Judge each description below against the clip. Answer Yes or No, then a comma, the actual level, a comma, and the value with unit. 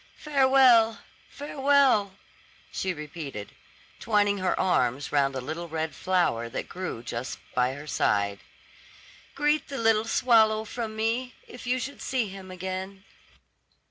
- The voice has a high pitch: Yes, high, 200 Hz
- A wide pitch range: Yes, wide, 7.7 semitones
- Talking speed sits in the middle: No, slow, 130 wpm